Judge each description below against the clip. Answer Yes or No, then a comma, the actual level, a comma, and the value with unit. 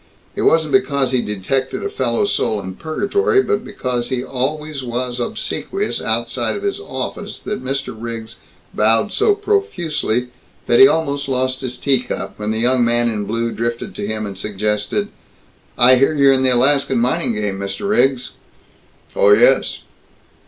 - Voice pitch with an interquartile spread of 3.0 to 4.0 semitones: No, wide, 5.5 semitones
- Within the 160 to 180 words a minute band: Yes, average, 165 wpm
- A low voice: Yes, low, 130 Hz